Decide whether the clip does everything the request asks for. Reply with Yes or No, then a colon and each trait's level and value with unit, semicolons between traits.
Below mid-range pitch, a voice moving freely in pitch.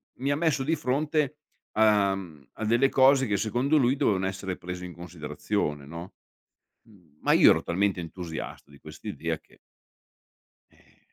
Yes: low, 100 Hz; wide, 7.3 semitones